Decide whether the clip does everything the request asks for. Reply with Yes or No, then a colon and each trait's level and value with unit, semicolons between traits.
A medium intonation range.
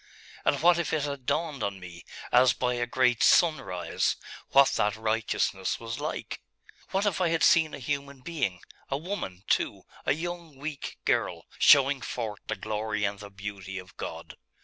No: wide, 6.6 semitones